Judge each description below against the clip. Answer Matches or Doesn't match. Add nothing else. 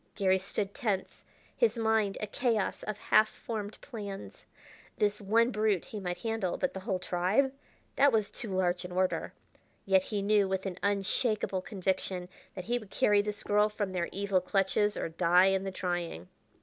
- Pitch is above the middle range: Matches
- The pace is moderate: Matches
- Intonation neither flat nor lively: Doesn't match